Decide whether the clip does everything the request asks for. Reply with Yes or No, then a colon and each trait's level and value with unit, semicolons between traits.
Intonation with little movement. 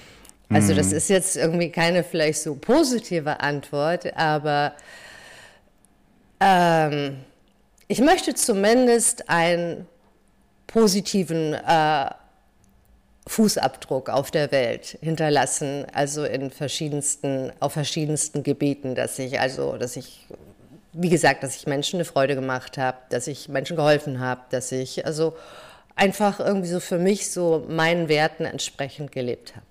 No: average, 3.9 semitones